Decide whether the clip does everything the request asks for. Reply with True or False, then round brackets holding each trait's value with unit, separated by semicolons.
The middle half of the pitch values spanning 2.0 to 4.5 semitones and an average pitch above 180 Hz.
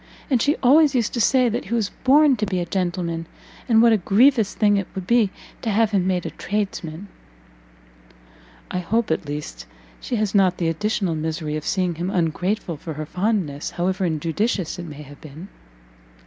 False (5.0 semitones; 190 Hz)